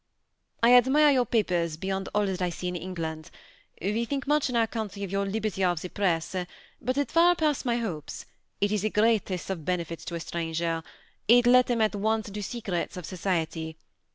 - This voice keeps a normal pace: No, fast, 210 wpm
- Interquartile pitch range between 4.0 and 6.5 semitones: Yes, average, 5.1 semitones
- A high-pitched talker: Yes, high, 200 Hz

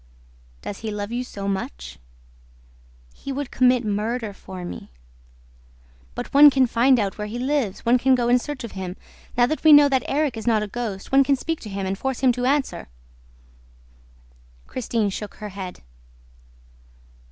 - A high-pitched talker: Yes, high, 240 Hz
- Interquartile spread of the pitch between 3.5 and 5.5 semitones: Yes, average, 4.6 semitones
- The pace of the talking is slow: No, average, 175 wpm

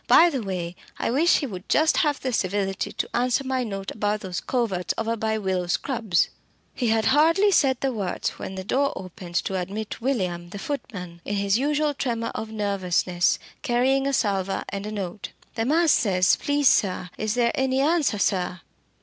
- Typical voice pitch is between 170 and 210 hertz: No, high, 220 Hz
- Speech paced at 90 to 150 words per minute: No, average, 185 wpm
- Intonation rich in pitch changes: Yes, wide, 5.8 semitones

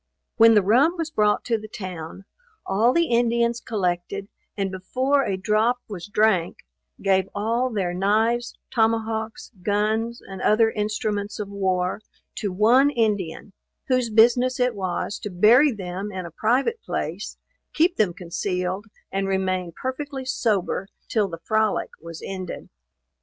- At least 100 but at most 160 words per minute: Yes, average, 140 wpm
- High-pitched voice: Yes, high, 210 Hz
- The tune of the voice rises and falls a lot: No, average, 3.6 semitones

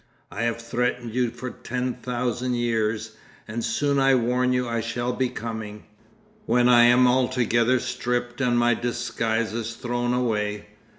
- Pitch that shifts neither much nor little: No, narrow, 1.3 semitones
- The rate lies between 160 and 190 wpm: No, average, 150 wpm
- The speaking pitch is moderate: No, low, 120 Hz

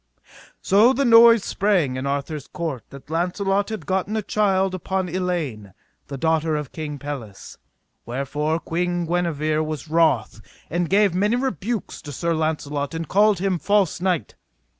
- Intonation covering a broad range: No, average, 4.6 semitones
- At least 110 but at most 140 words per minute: No, average, 150 wpm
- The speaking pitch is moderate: Yes, medium, 170 Hz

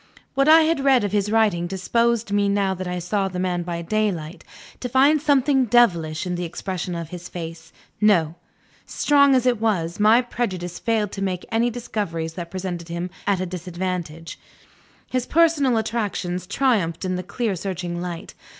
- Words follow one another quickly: No, average, 175 wpm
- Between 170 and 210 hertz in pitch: Yes, high, 190 Hz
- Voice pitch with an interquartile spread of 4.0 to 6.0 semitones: Yes, average, 5.0 semitones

